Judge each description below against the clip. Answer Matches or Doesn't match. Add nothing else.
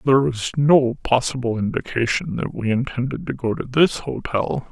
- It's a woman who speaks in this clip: Doesn't match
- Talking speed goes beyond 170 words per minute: Doesn't match